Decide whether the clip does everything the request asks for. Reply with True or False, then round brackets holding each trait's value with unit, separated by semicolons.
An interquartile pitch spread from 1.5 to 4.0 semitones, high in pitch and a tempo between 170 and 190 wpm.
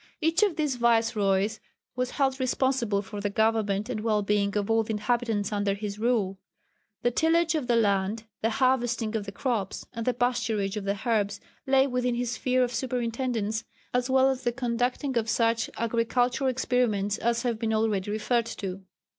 True (3.1 semitones; 230 Hz; 180 wpm)